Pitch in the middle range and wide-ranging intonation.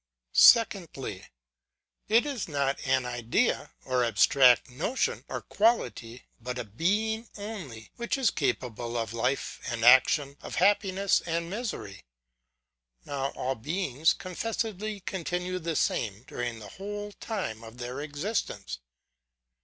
Yes: medium, 145 Hz; wide, 8.7 semitones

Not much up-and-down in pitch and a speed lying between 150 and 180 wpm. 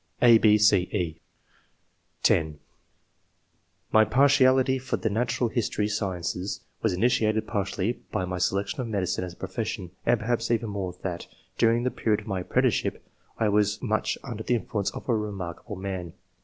No: average, 3.6 semitones; average, 160 wpm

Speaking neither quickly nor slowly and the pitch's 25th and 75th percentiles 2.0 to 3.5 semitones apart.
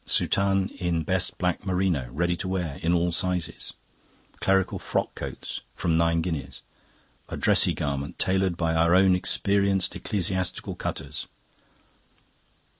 No: slow, 125 wpm; narrow, 2.4 semitones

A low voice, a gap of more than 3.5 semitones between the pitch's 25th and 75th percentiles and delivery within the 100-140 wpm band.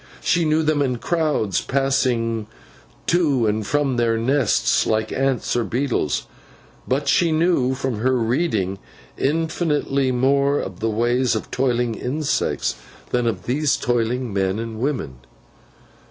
Yes: low, 125 Hz; average, 3.9 semitones; slow, 135 wpm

